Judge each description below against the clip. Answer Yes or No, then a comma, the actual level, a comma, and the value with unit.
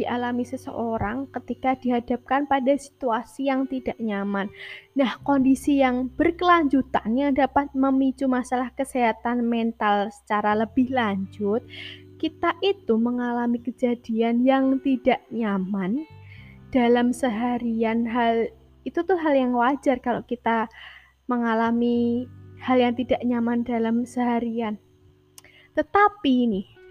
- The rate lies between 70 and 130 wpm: Yes, average, 105 wpm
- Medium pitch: No, high, 245 Hz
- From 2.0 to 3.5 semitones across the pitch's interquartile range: Yes, average, 2.7 semitones